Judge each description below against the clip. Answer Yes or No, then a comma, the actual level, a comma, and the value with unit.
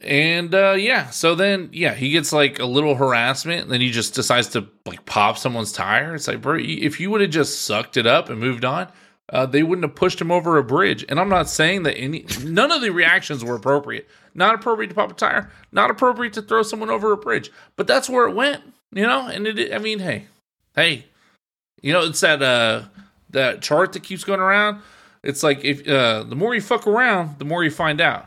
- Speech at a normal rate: No, fast, 230 wpm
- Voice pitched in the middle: Yes, medium, 160 Hz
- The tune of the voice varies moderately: No, wide, 6.4 semitones